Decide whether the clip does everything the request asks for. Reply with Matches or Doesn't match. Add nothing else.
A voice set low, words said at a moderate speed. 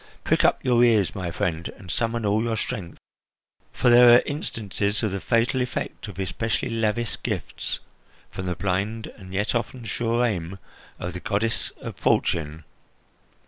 Matches